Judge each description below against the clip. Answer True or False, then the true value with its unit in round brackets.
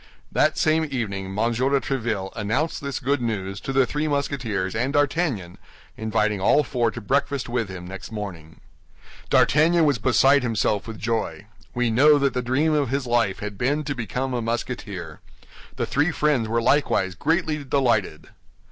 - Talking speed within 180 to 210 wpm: False (165 wpm)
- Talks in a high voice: False (120 Hz)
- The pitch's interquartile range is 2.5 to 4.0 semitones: False (5.0 semitones)